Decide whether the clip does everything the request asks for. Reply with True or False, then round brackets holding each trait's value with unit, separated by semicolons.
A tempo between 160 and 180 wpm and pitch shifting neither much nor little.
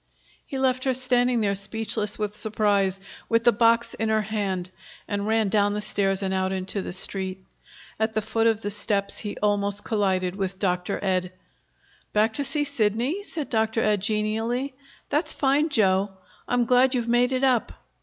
True (175 wpm; 3.4 semitones)